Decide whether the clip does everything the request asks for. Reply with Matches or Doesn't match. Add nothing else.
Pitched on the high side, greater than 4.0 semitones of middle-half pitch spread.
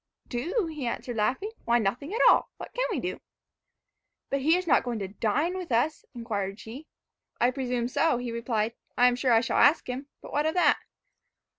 Matches